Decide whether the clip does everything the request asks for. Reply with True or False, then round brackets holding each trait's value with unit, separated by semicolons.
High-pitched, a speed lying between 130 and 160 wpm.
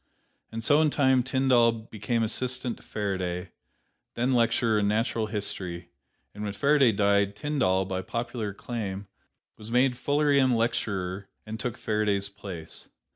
False (110 Hz; 135 wpm)